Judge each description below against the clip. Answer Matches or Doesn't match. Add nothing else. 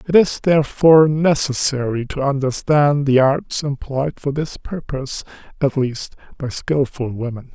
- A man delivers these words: Matches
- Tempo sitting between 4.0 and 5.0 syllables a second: Matches